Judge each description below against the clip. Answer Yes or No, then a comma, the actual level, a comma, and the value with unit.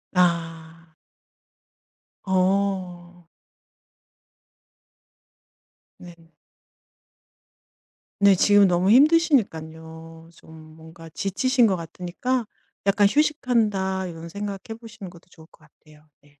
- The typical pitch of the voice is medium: Yes, medium, 180 Hz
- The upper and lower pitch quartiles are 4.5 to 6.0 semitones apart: No, average, 3.8 semitones